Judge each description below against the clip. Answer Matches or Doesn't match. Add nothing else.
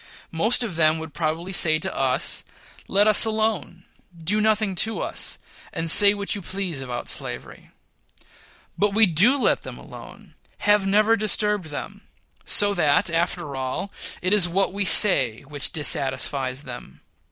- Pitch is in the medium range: Matches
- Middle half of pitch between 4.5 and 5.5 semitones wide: Matches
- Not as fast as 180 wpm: Matches